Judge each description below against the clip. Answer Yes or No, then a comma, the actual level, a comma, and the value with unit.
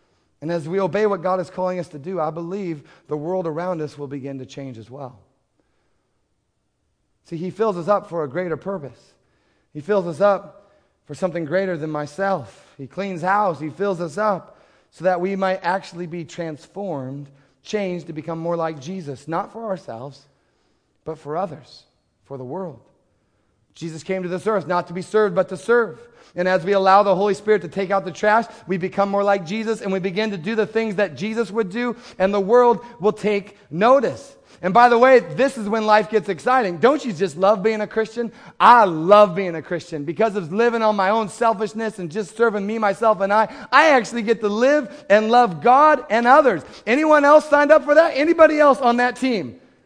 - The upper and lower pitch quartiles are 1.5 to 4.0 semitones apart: No, average, 4.6 semitones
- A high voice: Yes, high, 195 Hz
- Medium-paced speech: No, fast, 210 wpm